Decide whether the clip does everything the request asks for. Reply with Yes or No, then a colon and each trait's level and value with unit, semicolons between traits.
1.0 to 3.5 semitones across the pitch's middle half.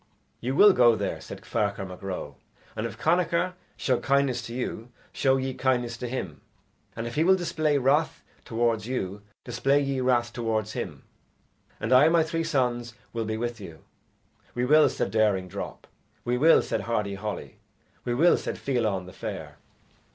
No: average, 4.2 semitones